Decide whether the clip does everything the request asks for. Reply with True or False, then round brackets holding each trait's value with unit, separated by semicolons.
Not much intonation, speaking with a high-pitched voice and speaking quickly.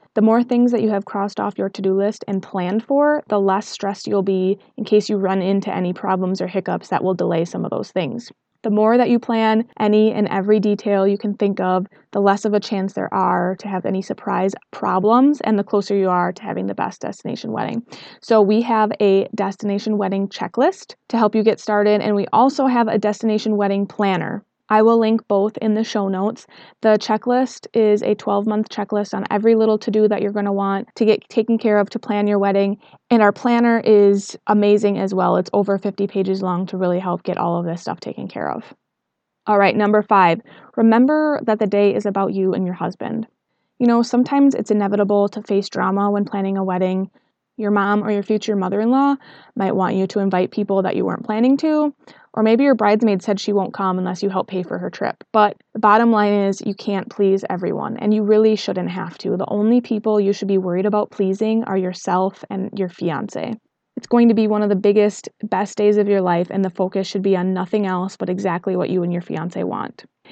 True (2.2 semitones; 205 Hz; 225 wpm)